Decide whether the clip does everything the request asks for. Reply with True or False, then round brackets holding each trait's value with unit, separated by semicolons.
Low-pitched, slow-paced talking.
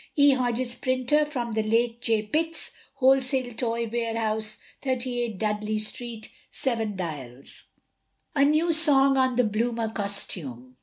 False (235 Hz; 125 wpm)